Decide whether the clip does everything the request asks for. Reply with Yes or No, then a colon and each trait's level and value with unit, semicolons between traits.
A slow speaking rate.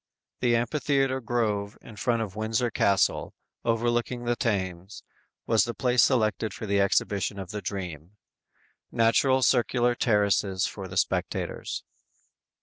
Yes: slow, 130 wpm